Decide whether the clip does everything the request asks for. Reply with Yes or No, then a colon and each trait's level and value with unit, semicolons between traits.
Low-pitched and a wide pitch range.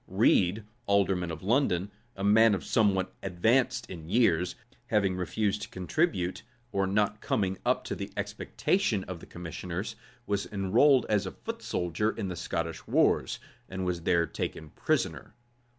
No: very low, 95 Hz; average, 3.0 semitones